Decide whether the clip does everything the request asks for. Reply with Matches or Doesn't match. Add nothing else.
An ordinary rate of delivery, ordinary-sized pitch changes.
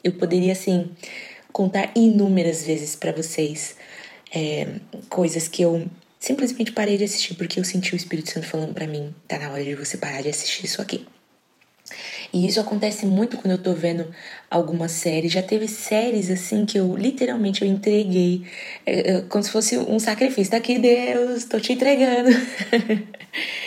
Matches